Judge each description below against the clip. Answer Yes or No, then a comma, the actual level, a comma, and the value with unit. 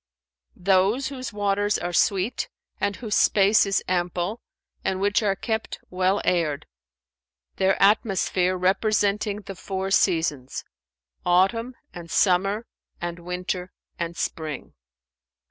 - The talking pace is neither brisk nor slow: No, slow, 110 wpm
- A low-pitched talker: No, high, 190 Hz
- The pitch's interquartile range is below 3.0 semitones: Yes, narrow, 2.6 semitones